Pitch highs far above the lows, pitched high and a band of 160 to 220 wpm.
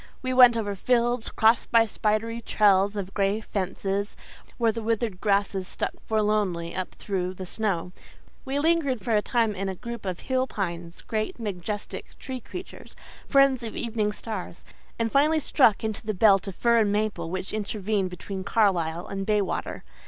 No: average, 3.2 semitones; high, 210 Hz; average, 165 wpm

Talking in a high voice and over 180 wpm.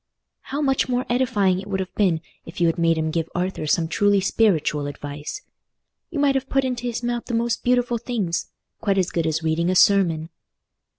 Yes: high, 195 Hz; average, 195 wpm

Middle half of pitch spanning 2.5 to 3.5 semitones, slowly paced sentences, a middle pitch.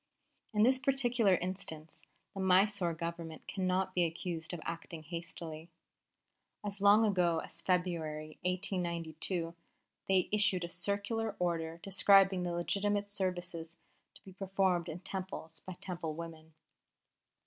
Yes: average, 2.8 semitones; slow, 125 wpm; medium, 180 Hz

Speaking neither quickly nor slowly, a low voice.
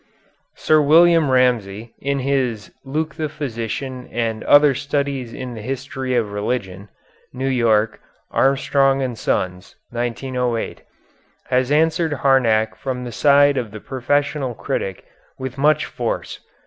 No: slow, 125 wpm; low, 130 Hz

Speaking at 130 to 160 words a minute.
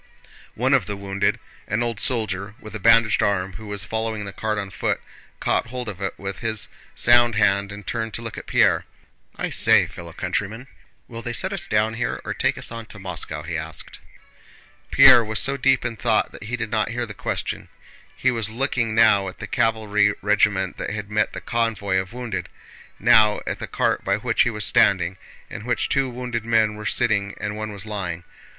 No: fast, 205 wpm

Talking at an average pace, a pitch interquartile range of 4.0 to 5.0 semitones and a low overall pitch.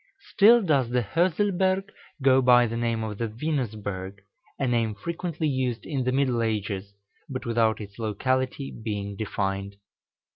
Yes: average, 145 wpm; average, 4.6 semitones; low, 120 Hz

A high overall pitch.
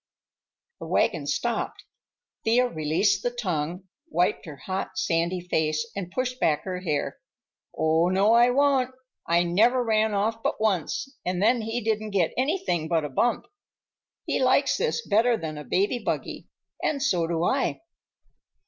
Yes: high, 200 Hz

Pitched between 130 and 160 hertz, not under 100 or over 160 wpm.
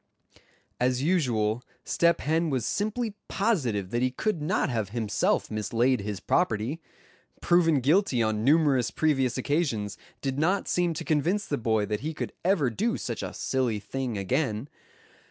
Yes: low, 135 Hz; average, 155 wpm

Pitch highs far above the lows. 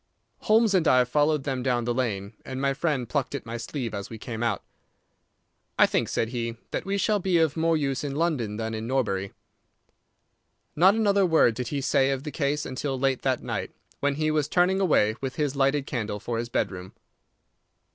No: average, 4.6 semitones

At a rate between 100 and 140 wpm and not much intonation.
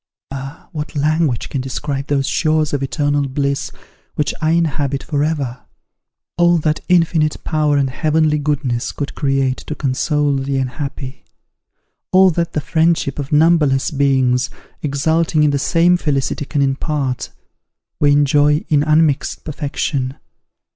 Yes: slow, 135 wpm; narrow, 2.3 semitones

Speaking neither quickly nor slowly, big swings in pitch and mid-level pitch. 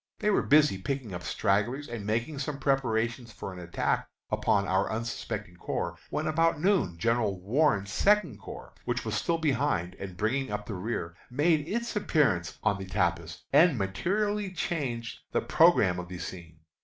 No: average, 165 wpm; wide, 8.1 semitones; low, 115 Hz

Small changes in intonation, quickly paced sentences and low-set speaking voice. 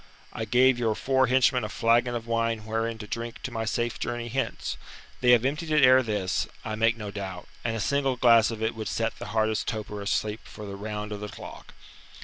Yes: narrow, 2.2 semitones; fast, 220 wpm; low, 115 Hz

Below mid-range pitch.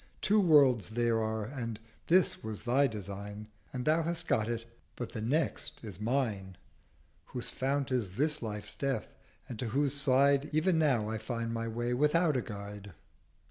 Yes: low, 120 Hz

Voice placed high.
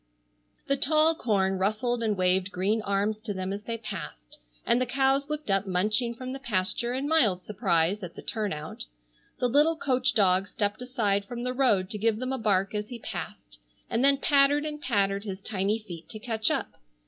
Yes: high, 215 Hz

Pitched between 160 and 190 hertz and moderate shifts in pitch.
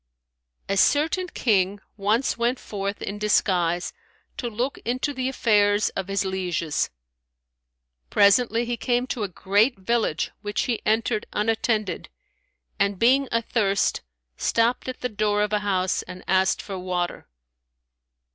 No: high, 210 Hz; average, 3.5 semitones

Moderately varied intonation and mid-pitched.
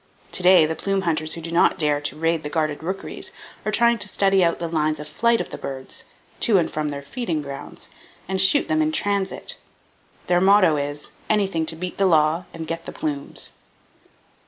Yes: average, 4.1 semitones; medium, 165 Hz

